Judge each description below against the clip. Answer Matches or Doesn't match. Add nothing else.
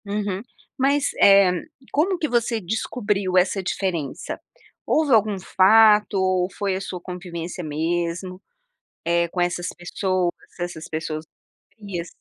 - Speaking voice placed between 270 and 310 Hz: Doesn't match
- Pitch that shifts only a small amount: Doesn't match